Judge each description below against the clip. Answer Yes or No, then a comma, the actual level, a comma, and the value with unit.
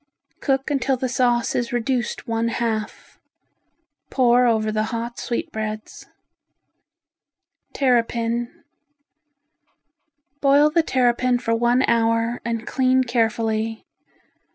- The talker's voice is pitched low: No, high, 235 Hz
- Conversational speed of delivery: No, slow, 95 wpm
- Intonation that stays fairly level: Yes, narrow, 1.9 semitones